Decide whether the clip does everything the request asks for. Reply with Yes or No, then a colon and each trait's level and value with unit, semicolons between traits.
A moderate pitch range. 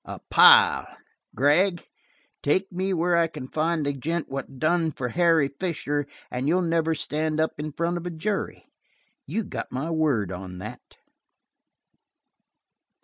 Yes: average, 3.2 semitones